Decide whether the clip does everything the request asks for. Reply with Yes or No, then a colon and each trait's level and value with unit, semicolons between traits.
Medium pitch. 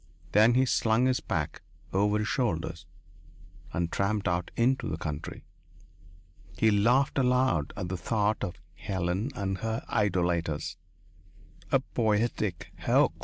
No: low, 105 Hz